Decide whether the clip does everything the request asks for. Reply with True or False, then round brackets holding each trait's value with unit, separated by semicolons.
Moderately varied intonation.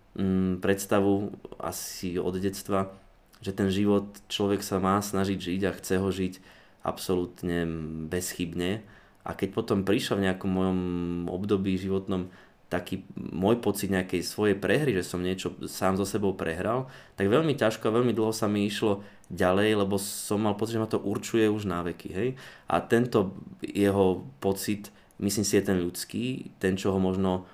False (1.9 semitones)